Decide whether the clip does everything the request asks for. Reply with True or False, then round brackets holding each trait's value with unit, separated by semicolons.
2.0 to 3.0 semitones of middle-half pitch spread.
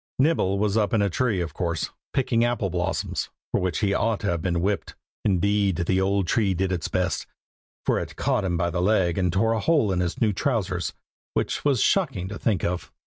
False (3.9 semitones)